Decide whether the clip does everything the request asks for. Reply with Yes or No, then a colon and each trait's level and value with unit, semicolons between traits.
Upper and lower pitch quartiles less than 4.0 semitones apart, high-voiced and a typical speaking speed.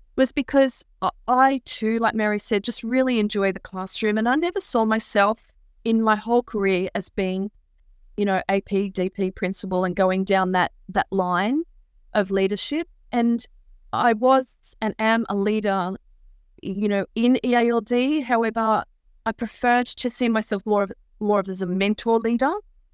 Yes: average, 3.6 semitones; high, 215 Hz; average, 160 wpm